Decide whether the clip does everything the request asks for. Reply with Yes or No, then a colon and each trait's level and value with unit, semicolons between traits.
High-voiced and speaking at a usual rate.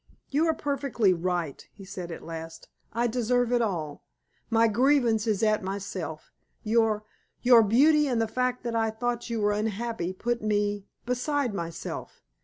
Yes: high, 225 Hz; average, 160 wpm